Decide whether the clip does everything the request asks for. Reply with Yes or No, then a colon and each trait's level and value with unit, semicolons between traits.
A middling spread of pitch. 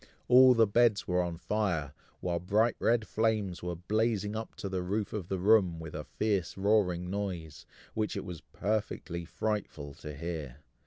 Yes: average, 4.0 semitones